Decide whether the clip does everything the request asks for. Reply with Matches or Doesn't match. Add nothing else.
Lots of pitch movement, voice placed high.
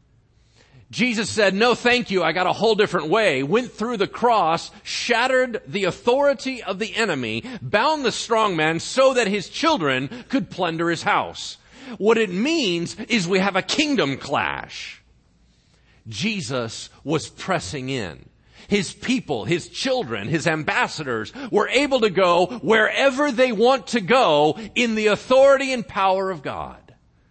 Matches